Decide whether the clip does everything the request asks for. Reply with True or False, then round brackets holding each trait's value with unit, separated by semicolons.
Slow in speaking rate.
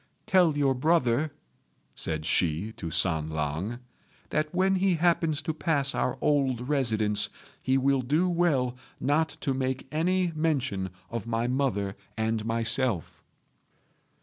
True (130 wpm)